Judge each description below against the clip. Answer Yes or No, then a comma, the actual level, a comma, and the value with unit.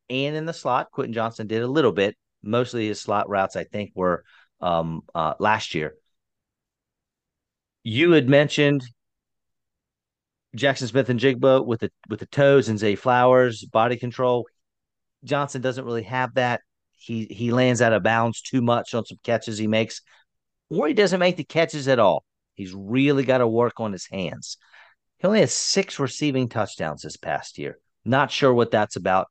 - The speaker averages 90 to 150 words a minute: No, average, 175 wpm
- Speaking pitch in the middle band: No, low, 125 Hz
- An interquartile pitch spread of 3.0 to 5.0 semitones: Yes, average, 3.4 semitones